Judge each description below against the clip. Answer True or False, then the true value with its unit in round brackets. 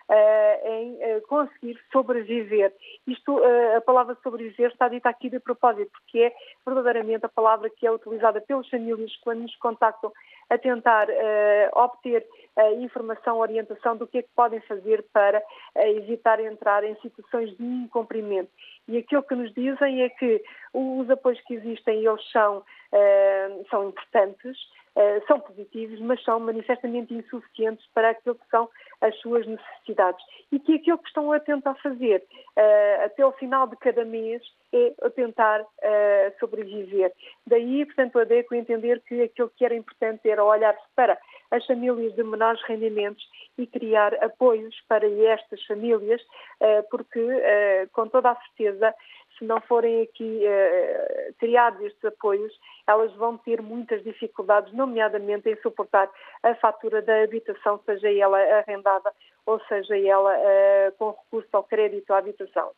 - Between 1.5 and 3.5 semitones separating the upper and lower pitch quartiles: True (2.9 semitones)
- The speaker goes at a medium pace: True (155 wpm)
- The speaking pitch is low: False (230 Hz)